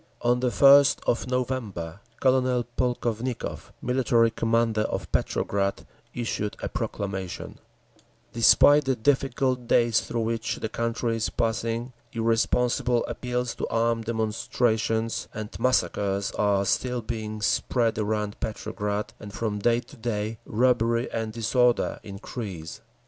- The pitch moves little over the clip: Yes, narrow, 2.3 semitones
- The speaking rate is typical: No, slow, 120 wpm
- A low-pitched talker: Yes, low, 115 Hz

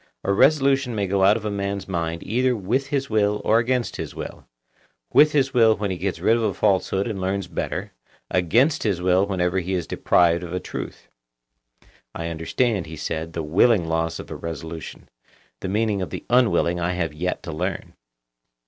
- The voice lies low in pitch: Yes, very low, 95 Hz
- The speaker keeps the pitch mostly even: No, average, 4.7 semitones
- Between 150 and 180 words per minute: No, average, 195 wpm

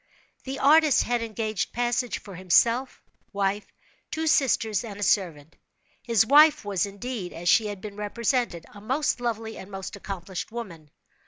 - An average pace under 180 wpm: Yes, average, 155 wpm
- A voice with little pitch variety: No, average, 3.9 semitones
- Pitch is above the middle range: Yes, high, 215 Hz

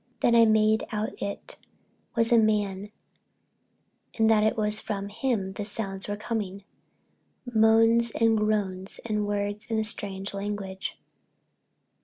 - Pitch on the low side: No, high, 210 Hz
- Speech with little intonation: Yes, narrow, 1.8 semitones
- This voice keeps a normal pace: No, slow, 130 wpm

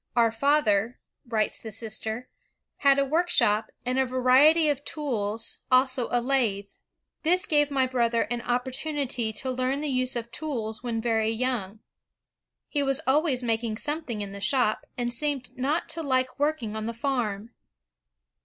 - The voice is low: No, very high, 250 Hz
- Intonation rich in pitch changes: No, average, 3.7 semitones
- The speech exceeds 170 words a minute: No, average, 160 wpm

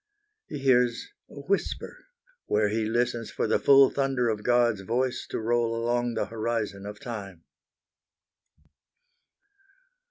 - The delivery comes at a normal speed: No, slow, 125 wpm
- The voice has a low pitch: Yes, low, 120 Hz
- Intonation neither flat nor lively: No, narrow, 2.2 semitones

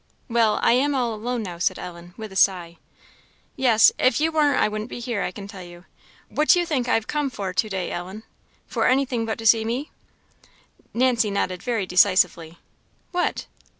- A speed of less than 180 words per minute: No, average, 195 wpm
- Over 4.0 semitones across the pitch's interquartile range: Yes, average, 5.2 semitones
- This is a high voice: Yes, high, 220 Hz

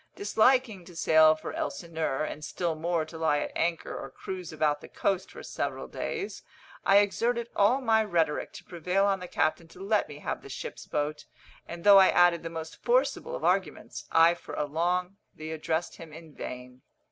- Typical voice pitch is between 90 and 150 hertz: No, medium, 170 Hz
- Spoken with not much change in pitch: No, average, 3.8 semitones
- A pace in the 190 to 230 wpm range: Yes, average, 195 wpm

